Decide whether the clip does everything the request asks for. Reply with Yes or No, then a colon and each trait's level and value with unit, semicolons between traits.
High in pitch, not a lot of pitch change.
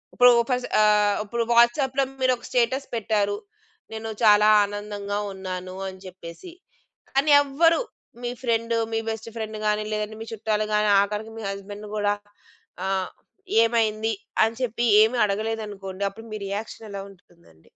Yes: high, 215 Hz; narrow, 2.3 semitones